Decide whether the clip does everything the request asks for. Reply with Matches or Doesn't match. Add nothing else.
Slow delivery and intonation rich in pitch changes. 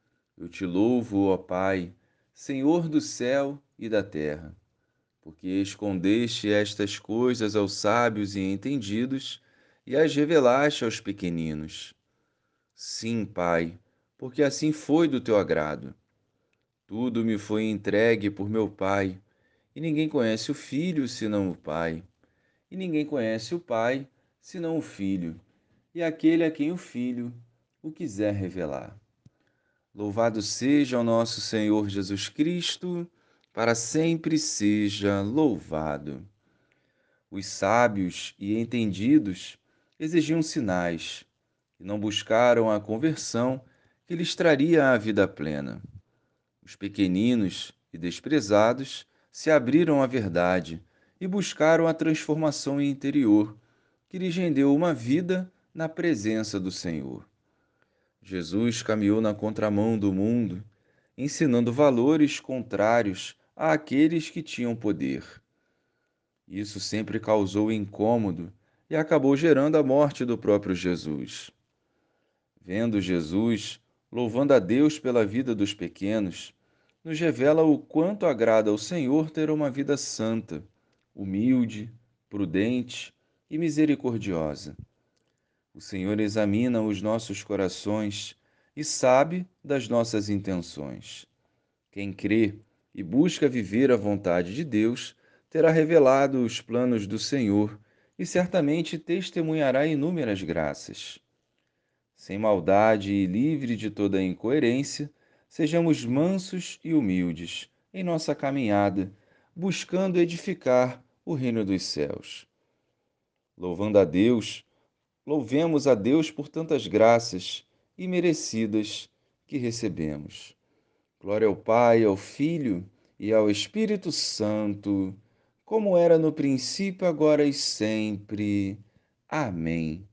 Matches